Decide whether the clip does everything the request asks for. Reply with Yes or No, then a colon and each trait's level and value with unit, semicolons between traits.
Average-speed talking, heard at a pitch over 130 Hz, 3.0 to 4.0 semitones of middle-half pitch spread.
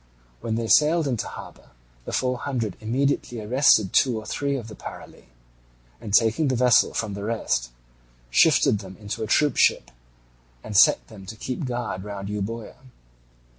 No: average, 160 wpm; low, 115 Hz; average, 3.7 semitones